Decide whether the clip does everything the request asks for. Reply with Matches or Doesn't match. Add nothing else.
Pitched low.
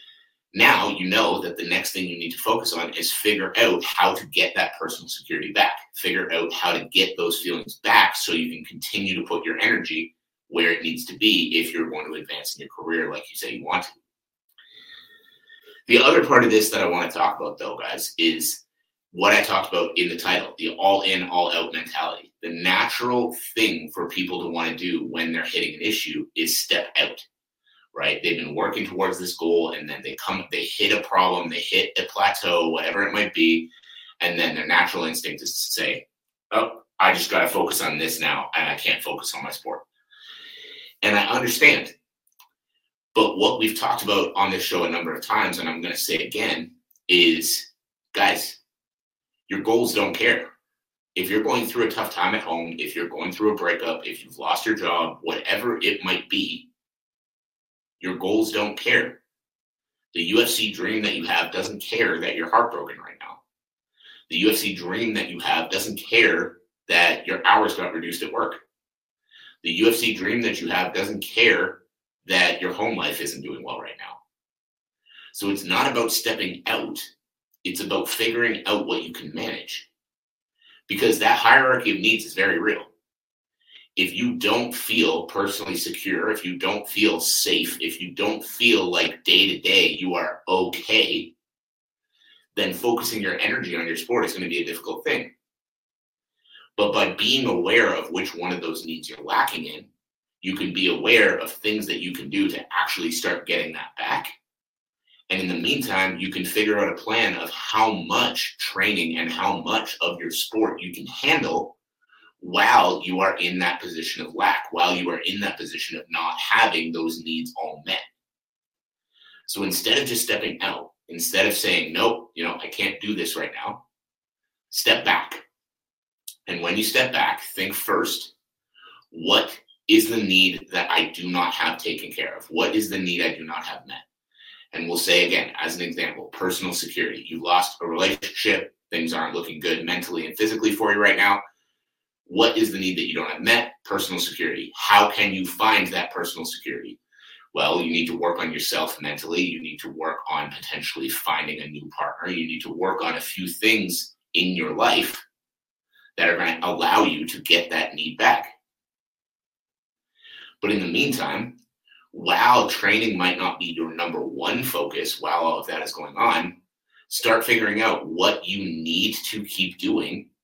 Matches